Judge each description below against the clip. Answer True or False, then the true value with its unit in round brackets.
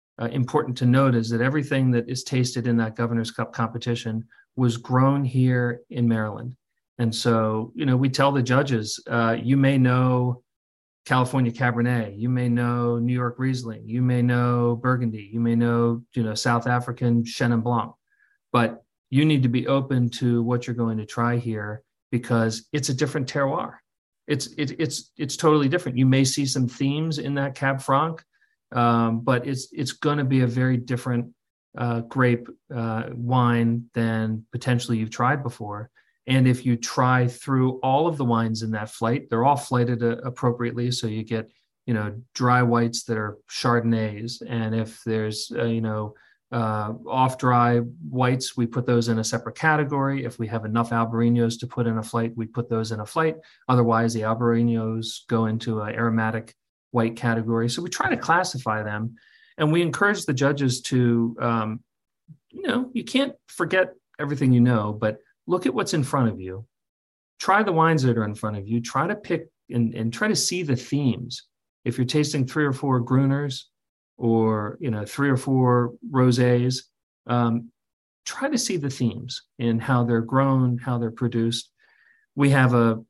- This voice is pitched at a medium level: False (120 Hz)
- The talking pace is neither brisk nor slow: True (180 wpm)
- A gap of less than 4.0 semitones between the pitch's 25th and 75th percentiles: True (2.5 semitones)